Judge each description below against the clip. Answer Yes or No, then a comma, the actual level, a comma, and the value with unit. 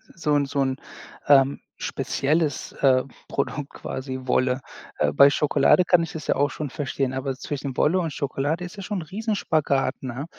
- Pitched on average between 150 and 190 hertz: No, medium, 140 Hz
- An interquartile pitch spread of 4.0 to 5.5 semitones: No, average, 3.0 semitones